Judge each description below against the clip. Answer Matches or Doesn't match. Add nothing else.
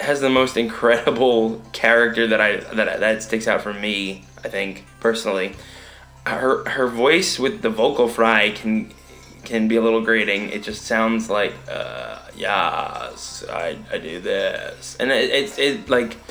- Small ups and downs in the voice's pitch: Matches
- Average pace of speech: Matches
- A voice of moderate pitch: Doesn't match